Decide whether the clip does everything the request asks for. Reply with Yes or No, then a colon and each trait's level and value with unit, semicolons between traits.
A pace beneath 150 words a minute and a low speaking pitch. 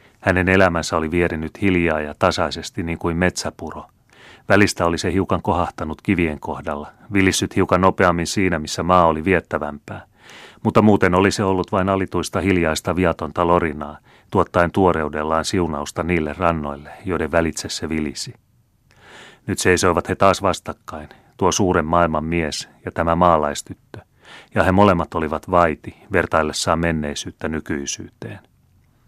Yes: average, 130 wpm; very low, 85 Hz